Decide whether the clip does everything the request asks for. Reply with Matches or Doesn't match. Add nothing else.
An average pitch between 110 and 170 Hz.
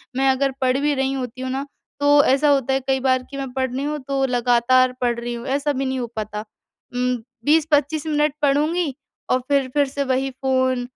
Doesn't match